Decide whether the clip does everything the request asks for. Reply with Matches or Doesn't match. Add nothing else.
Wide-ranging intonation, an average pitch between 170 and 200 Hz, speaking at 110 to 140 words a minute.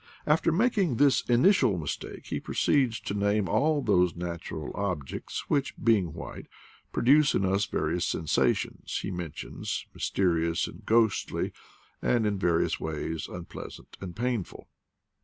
Doesn't match